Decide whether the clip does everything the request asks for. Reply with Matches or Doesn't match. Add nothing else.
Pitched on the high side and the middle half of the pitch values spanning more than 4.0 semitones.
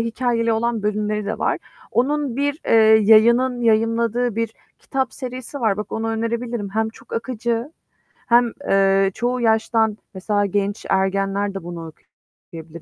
Doesn't match